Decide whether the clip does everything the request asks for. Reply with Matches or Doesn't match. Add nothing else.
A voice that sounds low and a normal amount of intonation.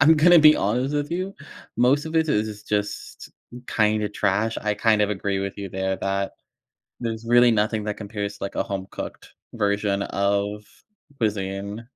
Matches